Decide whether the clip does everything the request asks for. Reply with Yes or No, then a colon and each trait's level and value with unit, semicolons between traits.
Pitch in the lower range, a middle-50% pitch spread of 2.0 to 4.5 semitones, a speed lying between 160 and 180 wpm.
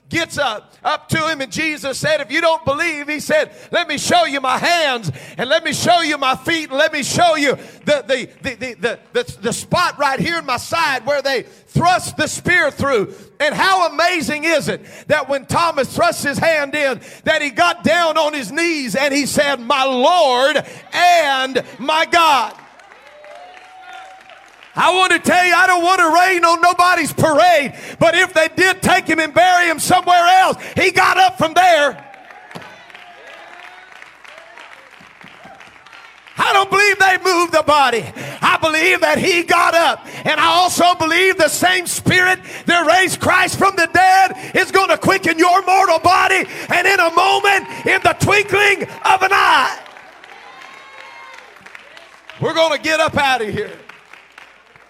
No: very high, 335 Hz; average, 3.5 semitones; average, 175 wpm